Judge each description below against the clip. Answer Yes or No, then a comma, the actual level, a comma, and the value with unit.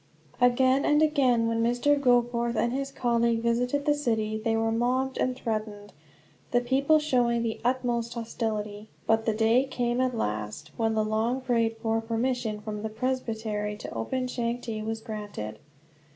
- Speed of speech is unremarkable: Yes, average, 160 wpm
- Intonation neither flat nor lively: No, narrow, 2.3 semitones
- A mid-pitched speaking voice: No, high, 235 Hz